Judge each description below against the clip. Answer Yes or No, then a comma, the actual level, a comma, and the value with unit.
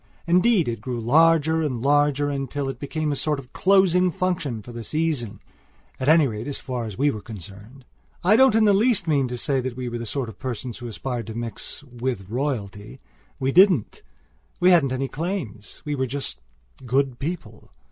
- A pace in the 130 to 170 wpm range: No, average, 195 wpm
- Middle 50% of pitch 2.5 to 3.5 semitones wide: No, average, 5.2 semitones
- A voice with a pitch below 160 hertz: Yes, low, 135 Hz